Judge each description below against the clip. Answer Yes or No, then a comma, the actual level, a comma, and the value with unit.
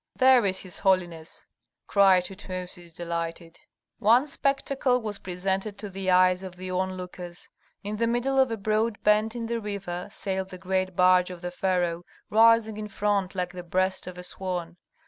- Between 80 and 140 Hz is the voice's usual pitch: No, high, 190 Hz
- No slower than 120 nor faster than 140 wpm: No, average, 170 wpm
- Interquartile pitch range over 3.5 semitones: No, average, 2.9 semitones